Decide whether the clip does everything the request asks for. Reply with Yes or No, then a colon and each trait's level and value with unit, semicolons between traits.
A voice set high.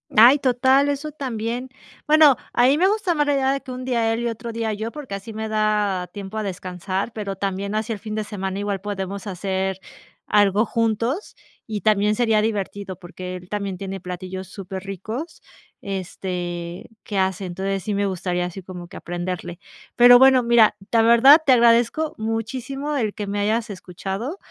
Yes: high, 210 Hz